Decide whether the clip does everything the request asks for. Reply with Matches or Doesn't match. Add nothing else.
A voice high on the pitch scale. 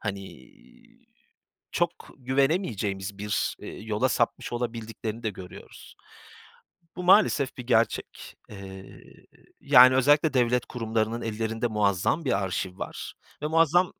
Doesn't match